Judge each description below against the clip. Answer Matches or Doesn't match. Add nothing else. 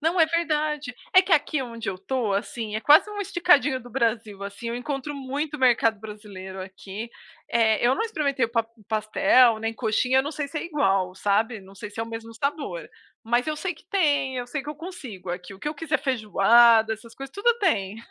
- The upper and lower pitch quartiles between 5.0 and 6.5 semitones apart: Matches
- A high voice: Matches